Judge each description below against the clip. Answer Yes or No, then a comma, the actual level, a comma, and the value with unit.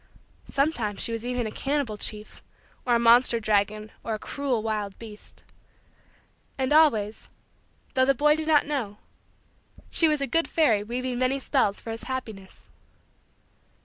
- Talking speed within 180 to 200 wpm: No, average, 150 wpm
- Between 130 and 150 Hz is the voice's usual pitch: No, high, 240 Hz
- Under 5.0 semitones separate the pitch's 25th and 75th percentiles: Yes, average, 4.4 semitones